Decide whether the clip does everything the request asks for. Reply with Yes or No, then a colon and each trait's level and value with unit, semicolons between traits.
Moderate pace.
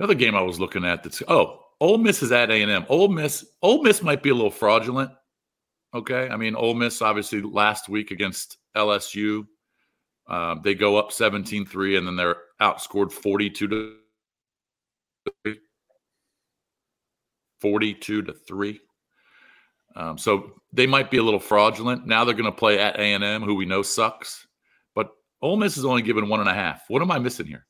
Yes: average, 170 wpm